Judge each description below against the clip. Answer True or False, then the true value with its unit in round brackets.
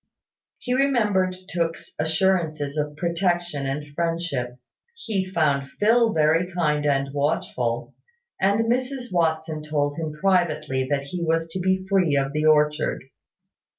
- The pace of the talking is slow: True (130 wpm)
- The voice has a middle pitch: True (165 Hz)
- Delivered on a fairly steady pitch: False (4.1 semitones)